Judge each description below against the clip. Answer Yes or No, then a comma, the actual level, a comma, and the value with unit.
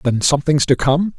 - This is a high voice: No, medium, 145 Hz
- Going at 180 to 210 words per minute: Yes, fast, 205 wpm